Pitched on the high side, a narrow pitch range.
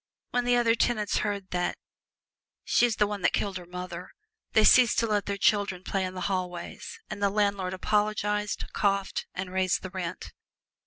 Yes: high, 200 Hz; narrow, 2.3 semitones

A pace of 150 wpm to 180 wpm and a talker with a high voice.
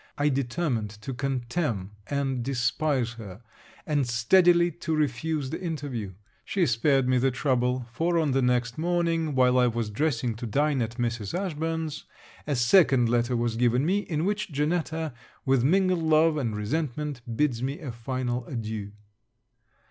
No: average, 155 wpm; low, 135 Hz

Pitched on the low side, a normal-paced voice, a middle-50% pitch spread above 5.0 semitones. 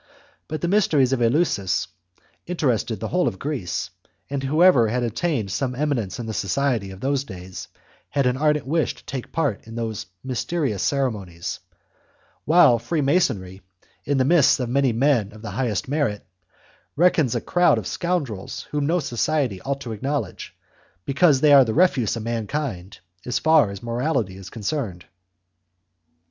Yes: low, 130 Hz; average, 160 wpm; wide, 5.4 semitones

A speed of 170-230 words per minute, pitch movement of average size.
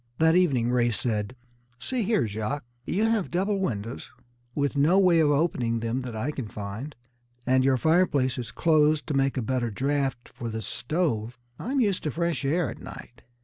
No: average, 185 wpm; wide, 5.9 semitones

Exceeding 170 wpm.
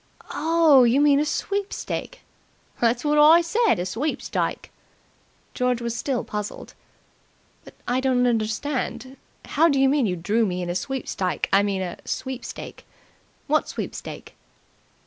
No: average, 140 wpm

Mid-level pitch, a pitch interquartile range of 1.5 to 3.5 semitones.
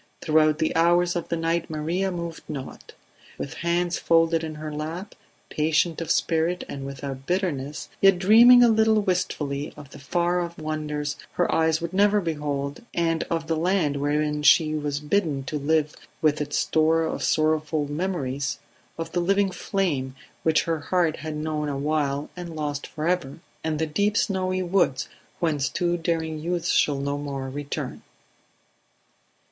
Yes: medium, 160 Hz; average, 2.9 semitones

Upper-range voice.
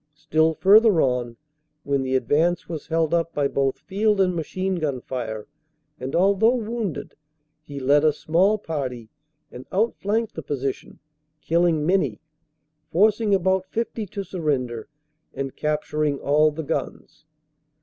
No: medium, 160 Hz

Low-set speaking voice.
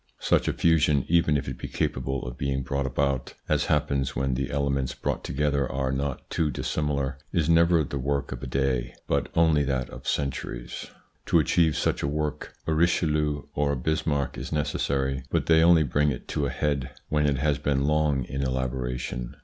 Yes: very low, 70 Hz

